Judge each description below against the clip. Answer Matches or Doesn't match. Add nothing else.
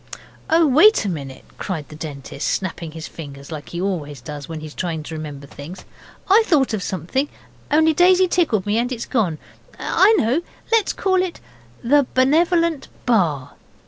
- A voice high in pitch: Matches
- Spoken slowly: Doesn't match